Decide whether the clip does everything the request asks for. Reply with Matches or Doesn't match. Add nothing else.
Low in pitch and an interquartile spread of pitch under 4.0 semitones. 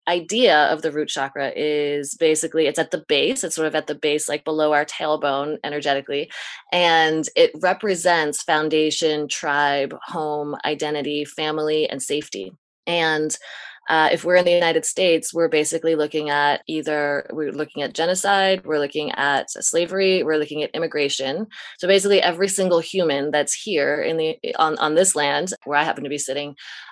Doesn't match